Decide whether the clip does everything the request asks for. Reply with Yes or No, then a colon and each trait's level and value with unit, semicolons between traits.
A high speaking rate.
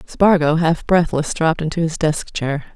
No: average, 175 wpm